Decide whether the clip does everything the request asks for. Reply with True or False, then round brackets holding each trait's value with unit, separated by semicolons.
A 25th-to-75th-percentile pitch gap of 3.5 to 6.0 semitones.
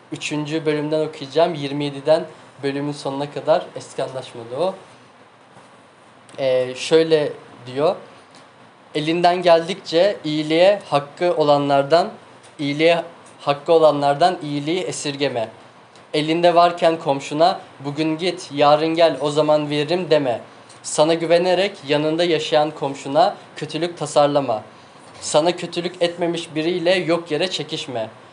False (2.7 semitones)